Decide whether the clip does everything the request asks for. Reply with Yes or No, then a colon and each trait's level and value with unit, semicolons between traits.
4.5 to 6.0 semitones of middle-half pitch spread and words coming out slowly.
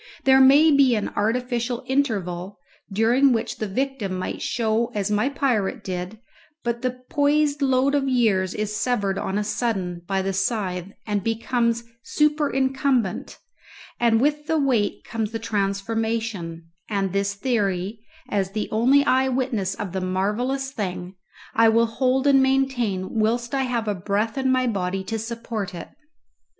No: average, 4.8 semitones; average, 150 wpm